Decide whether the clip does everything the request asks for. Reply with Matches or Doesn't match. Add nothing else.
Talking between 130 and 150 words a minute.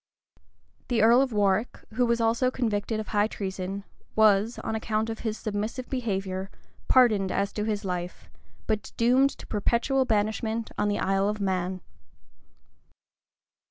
Matches